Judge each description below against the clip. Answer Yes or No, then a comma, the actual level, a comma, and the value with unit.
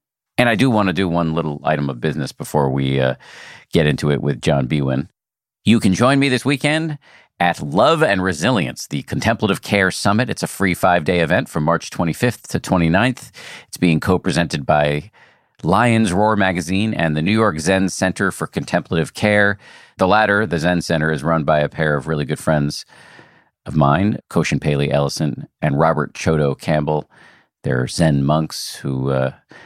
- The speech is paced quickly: No, average, 180 wpm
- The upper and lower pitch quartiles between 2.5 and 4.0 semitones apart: No, wide, 5.6 semitones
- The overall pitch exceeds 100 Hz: No, very low, 80 Hz